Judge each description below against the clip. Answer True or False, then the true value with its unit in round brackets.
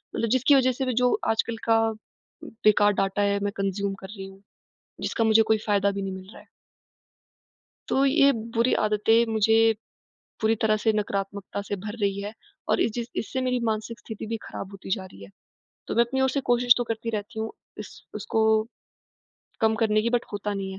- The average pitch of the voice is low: False (220 Hz)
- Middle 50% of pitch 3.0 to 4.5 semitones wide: False (2.6 semitones)